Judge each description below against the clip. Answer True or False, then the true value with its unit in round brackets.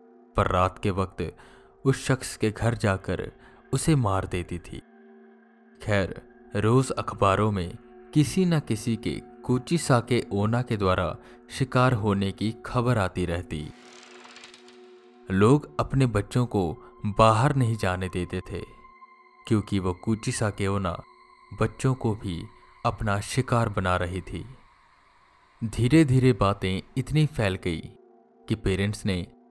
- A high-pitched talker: False (110 Hz)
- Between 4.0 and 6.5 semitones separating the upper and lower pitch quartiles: True (4.6 semitones)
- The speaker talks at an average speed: False (130 wpm)